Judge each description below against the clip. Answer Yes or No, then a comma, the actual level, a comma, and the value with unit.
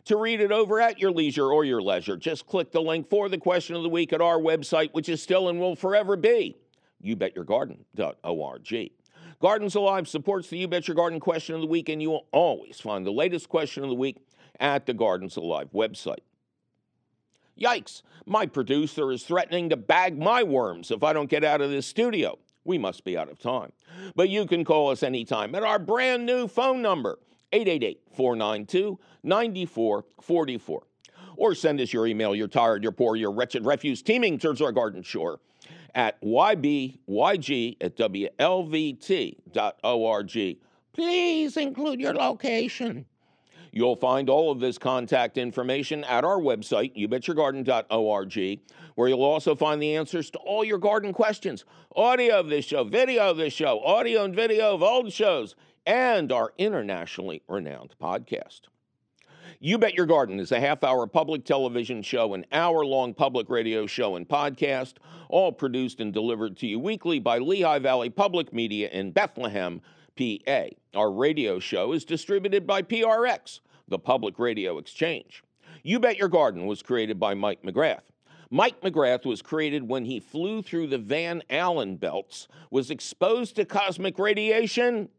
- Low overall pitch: No, medium, 165 Hz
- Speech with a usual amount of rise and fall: No, wide, 7.6 semitones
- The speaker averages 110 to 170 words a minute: Yes, average, 165 wpm